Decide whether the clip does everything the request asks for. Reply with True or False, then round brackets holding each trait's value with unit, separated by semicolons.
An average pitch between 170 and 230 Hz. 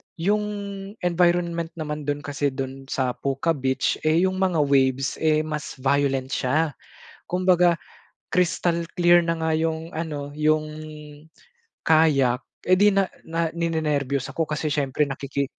False (155 Hz)